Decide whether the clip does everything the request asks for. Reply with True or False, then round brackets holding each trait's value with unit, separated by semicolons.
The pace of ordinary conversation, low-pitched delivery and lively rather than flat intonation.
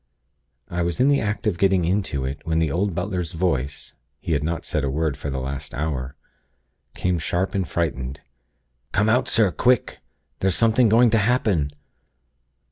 True (175 wpm; 85 Hz; 6.1 semitones)